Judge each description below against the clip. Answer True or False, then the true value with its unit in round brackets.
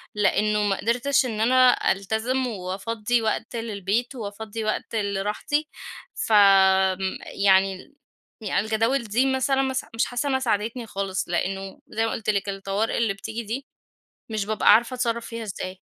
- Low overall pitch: False (220 Hz)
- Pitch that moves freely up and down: False (3.1 semitones)